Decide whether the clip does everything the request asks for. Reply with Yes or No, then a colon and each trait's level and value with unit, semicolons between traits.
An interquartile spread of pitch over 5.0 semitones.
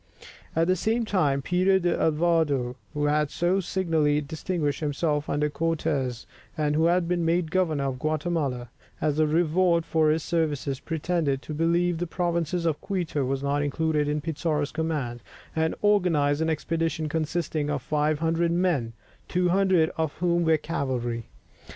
No: average, 2.7 semitones